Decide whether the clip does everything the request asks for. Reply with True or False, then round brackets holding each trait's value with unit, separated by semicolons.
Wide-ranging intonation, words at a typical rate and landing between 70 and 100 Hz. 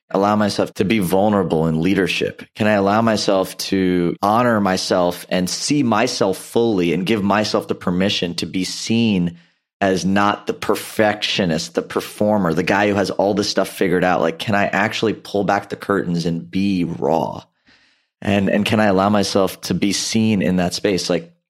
False (2.7 semitones; 180 wpm; 95 Hz)